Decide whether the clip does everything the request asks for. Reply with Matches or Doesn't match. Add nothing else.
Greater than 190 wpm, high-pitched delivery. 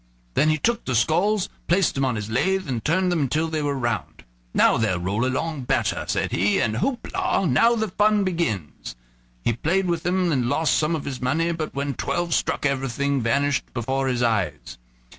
Doesn't match